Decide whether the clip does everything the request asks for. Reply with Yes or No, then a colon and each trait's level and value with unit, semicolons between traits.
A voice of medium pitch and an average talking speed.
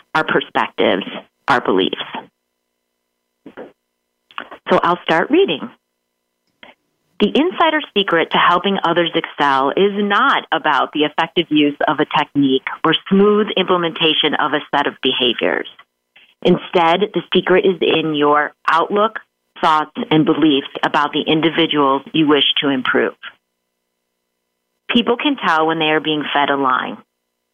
No: medium, 150 Hz; slow, 130 wpm